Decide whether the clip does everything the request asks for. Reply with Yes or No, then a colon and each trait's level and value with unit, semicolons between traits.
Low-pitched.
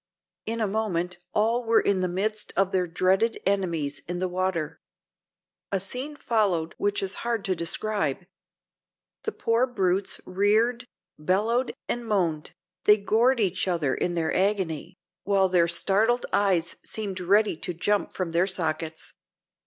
No: high, 195 Hz